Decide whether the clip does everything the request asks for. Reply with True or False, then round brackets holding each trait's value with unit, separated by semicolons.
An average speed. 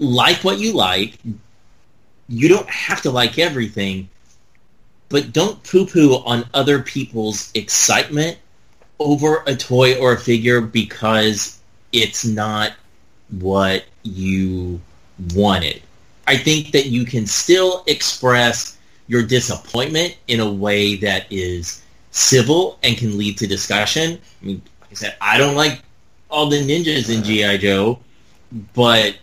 False (130 wpm)